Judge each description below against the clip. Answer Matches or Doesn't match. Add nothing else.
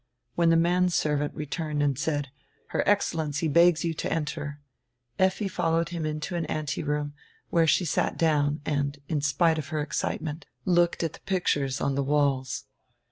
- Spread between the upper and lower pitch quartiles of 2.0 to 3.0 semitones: Matches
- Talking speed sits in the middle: Matches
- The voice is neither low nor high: Matches